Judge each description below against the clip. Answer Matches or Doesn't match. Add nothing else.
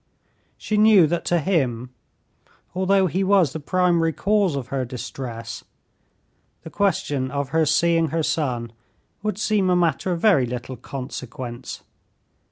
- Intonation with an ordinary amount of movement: Doesn't match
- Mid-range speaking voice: Matches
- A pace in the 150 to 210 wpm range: Doesn't match